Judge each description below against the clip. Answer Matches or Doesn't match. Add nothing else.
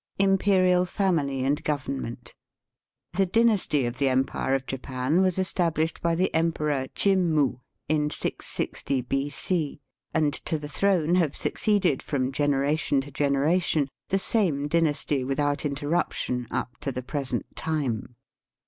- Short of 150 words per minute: Matches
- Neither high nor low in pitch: Matches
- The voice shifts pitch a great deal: Doesn't match